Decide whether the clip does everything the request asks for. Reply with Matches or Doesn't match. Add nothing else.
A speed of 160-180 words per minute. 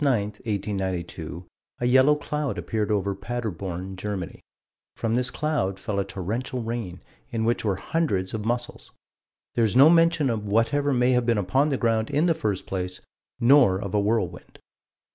Matches